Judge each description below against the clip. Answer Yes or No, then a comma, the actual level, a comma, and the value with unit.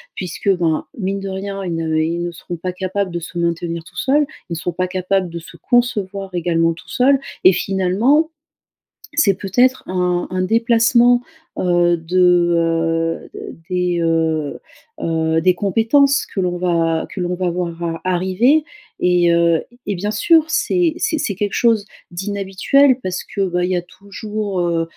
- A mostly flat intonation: No, average, 3.2 semitones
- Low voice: No, medium, 185 Hz